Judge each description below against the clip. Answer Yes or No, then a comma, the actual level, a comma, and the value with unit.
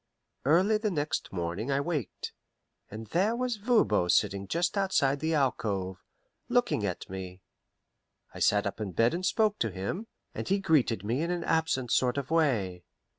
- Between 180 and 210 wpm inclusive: No, average, 170 wpm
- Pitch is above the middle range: No, medium, 140 Hz